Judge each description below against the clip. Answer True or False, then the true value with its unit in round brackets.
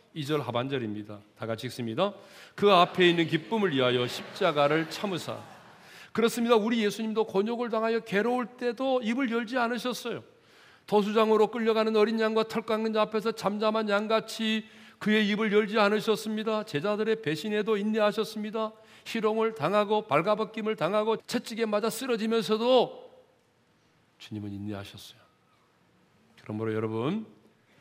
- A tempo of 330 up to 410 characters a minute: True (340 characters per minute)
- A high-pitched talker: True (215 Hz)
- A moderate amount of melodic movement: True (4.3 semitones)